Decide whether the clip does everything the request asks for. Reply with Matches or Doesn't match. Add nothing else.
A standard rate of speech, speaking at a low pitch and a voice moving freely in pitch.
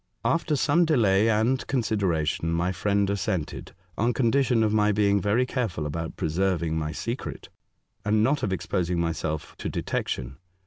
Matches